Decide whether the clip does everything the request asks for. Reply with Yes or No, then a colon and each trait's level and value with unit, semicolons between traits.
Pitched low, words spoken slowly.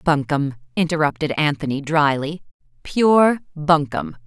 No: medium, 155 Hz; slow, 85 wpm